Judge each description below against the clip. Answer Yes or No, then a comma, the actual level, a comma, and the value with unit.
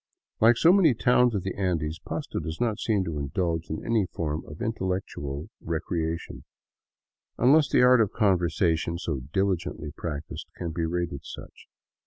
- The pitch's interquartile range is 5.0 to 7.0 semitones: Yes, wide, 5.4 semitones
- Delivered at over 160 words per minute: No, average, 155 wpm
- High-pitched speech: No, very low, 85 Hz